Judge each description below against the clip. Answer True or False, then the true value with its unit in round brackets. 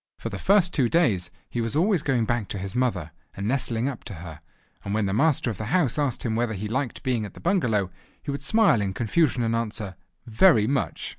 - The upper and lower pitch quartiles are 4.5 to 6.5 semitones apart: True (5.1 semitones)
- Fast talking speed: True (230 wpm)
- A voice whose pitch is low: True (115 Hz)